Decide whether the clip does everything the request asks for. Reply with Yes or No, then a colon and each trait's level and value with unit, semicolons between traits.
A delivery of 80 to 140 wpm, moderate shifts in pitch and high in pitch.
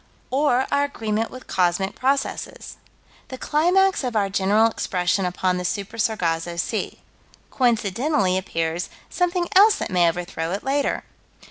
No: slow, 135 wpm; wide, 7.0 semitones; high, 210 Hz